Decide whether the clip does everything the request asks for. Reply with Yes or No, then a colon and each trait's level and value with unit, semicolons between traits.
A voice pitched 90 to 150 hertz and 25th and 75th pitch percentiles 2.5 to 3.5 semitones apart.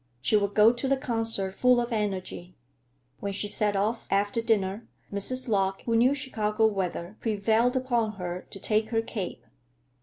No: high, 215 Hz; average, 2.9 semitones